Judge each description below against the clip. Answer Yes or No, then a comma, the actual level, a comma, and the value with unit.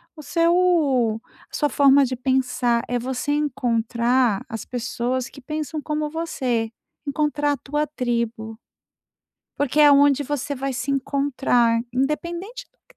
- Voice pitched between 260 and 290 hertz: Yes, very high, 270 Hz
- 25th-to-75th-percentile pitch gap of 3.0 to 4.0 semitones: Yes, average, 3.5 semitones